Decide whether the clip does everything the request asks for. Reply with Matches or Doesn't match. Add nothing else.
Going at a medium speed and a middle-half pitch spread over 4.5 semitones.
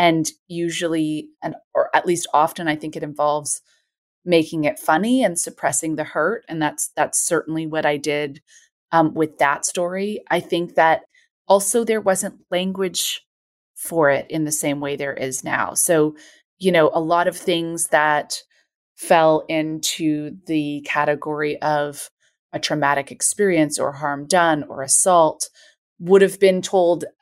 Doesn't match